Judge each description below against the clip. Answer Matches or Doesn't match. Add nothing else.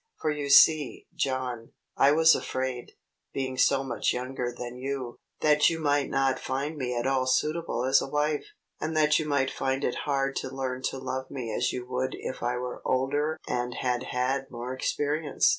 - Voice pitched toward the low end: Matches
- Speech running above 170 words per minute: Matches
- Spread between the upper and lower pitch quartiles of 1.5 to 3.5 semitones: Matches